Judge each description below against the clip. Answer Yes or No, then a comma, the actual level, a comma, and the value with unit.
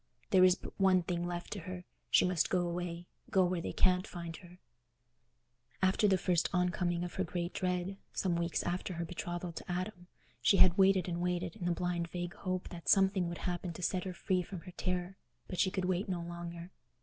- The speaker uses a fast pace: Yes, fast, 215 wpm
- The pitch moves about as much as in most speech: No, narrow, 1.2 semitones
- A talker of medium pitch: Yes, medium, 180 Hz